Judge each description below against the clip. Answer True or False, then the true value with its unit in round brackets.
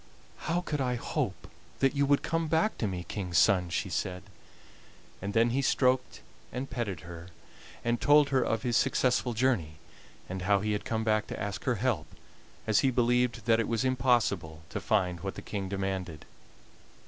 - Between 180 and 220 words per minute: True (185 wpm)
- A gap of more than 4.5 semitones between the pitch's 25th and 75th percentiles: True (5.2 semitones)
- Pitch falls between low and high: False (115 Hz)